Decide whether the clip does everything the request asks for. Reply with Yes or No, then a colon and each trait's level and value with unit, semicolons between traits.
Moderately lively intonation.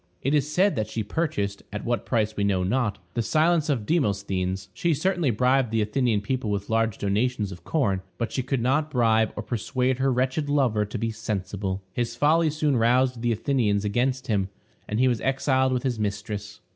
Yes: average, 4.3 semitones